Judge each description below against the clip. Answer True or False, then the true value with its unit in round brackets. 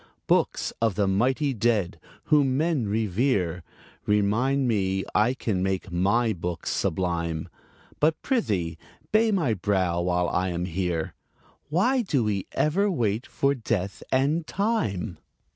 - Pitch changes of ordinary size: False (7.1 semitones)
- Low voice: True (105 Hz)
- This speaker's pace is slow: True (130 wpm)